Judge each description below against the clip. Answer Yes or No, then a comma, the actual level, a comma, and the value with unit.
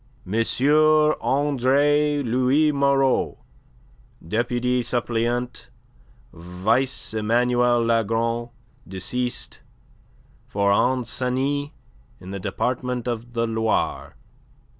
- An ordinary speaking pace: No, slow, 75 wpm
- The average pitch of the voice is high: No, low, 120 Hz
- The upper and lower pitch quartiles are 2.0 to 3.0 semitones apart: Yes, narrow, 2.4 semitones